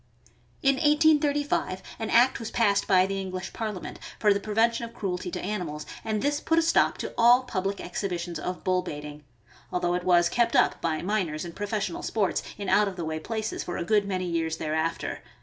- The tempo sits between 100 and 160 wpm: No, average, 200 wpm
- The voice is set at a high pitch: Yes, high, 195 Hz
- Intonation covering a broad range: No, average, 4.3 semitones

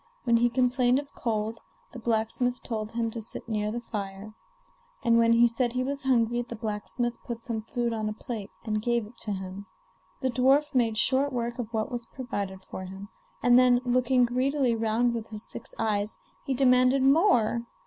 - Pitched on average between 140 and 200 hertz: No, high, 235 Hz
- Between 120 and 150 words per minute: No, average, 190 wpm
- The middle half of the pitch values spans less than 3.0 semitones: Yes, narrow, 2.5 semitones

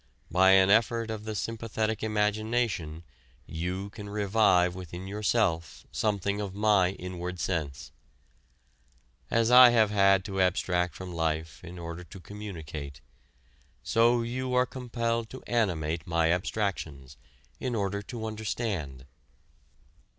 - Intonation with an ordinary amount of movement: Yes, average, 4.1 semitones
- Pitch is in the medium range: No, low, 100 Hz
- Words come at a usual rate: No, slow, 120 wpm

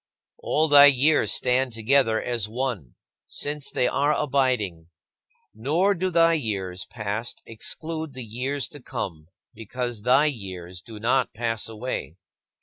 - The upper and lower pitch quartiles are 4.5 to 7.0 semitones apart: Yes, average, 4.8 semitones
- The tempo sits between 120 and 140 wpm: Yes, slow, 135 wpm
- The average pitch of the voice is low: Yes, low, 125 Hz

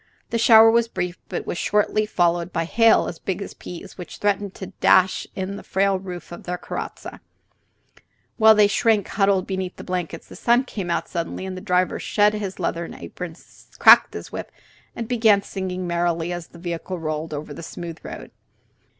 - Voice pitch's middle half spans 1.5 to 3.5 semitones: Yes, average, 3.1 semitones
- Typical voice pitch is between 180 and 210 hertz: Yes, medium, 185 Hz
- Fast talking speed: No, average, 185 wpm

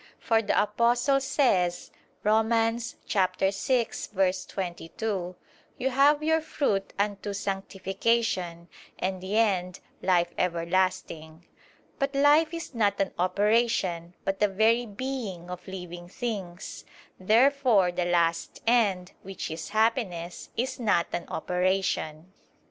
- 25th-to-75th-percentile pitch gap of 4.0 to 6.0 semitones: Yes, average, 4.4 semitones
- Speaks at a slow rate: Yes, slow, 110 wpm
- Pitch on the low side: No, high, 195 Hz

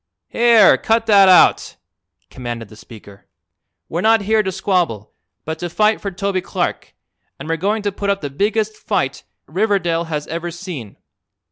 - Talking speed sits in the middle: Yes, average, 160 wpm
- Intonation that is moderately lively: Yes, average, 4.6 semitones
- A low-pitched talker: No, medium, 185 Hz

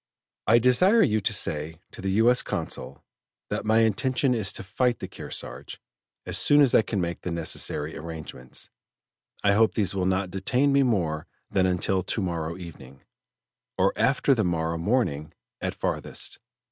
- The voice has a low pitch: Yes, very low, 95 Hz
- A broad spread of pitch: Yes, wide, 5.9 semitones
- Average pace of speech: Yes, average, 170 wpm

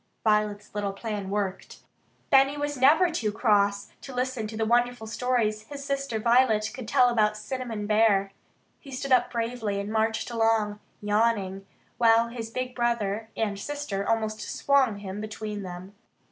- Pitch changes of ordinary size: Yes, average, 3.1 semitones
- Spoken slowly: No, average, 155 wpm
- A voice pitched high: Yes, high, 220 Hz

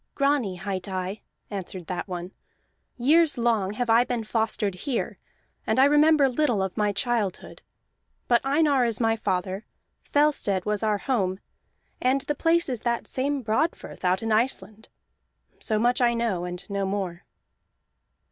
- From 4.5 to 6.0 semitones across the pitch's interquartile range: Yes, average, 5.1 semitones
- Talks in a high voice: Yes, high, 225 Hz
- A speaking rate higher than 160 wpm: No, average, 150 wpm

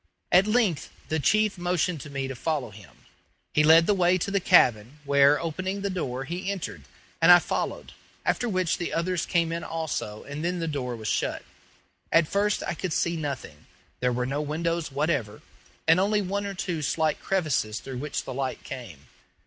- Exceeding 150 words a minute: Yes, average, 190 wpm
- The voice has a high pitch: No, medium, 160 Hz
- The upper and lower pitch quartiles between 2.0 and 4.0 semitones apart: No, average, 5.0 semitones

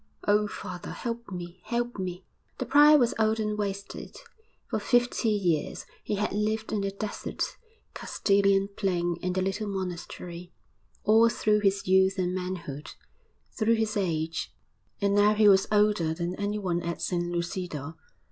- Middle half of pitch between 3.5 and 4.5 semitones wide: No, average, 3.1 semitones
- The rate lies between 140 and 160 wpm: Yes, average, 150 wpm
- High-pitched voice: Yes, high, 195 Hz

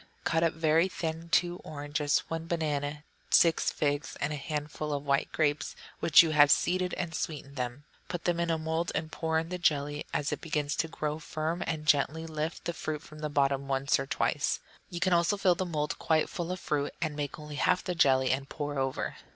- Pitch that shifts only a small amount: Yes, narrow, 2.3 semitones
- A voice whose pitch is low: No, medium, 155 Hz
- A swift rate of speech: Yes, fast, 215 wpm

